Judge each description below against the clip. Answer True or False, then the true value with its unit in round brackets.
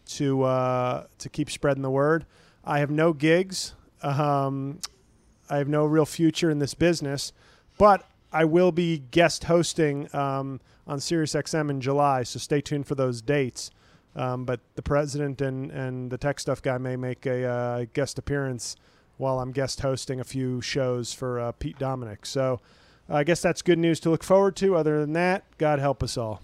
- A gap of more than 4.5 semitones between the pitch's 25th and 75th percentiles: False (3.3 semitones)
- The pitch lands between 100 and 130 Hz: False (140 Hz)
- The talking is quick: False (190 wpm)